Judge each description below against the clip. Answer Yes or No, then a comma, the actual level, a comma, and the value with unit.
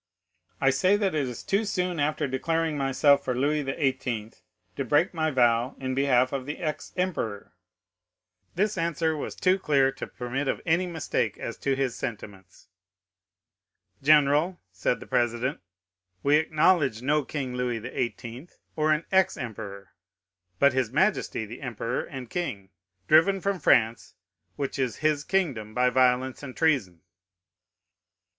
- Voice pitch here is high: No, medium, 140 Hz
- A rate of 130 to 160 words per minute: Yes, average, 145 wpm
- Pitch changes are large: No, average, 4.3 semitones